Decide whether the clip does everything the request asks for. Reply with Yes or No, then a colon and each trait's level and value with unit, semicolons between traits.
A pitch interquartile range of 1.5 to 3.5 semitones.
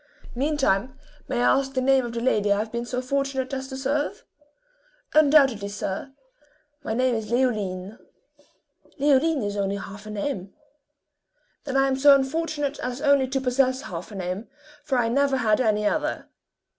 No: average, 4.4 semitones